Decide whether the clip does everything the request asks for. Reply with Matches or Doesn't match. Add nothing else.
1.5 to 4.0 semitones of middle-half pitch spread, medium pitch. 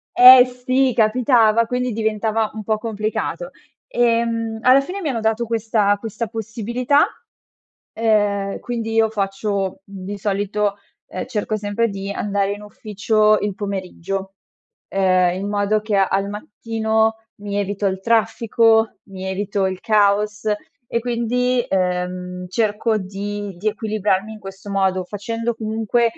Doesn't match